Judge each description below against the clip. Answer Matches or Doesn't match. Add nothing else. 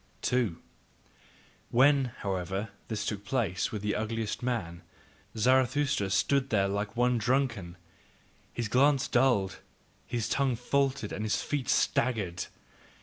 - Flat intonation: Doesn't match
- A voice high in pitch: Doesn't match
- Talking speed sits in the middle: Doesn't match